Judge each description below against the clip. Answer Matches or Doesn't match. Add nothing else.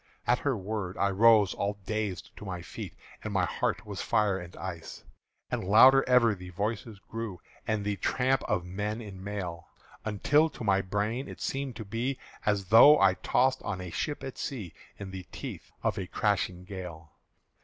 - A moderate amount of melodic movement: Matches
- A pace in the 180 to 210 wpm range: Matches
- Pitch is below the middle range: Matches